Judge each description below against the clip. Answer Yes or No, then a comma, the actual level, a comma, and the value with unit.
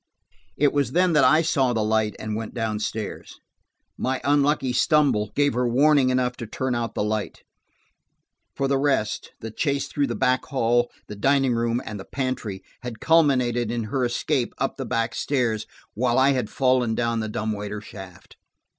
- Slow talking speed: No, average, 175 wpm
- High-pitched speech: No, low, 125 Hz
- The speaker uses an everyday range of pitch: Yes, average, 3.7 semitones